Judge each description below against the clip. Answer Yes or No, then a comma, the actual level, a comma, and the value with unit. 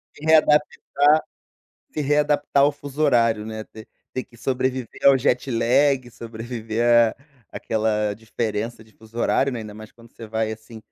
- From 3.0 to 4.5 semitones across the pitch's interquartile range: Yes, average, 3.7 semitones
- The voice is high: No, low, 120 Hz